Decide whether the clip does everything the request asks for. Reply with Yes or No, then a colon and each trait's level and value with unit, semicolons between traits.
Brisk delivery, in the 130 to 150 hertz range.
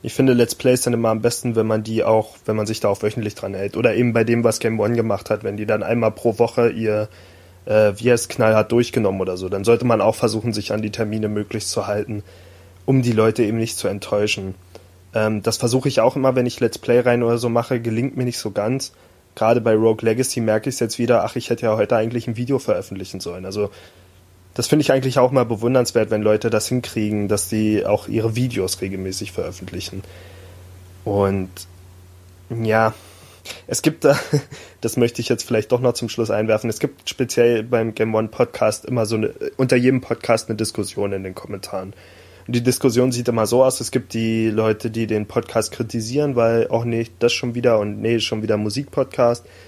No: fast, 215 wpm; low, 110 Hz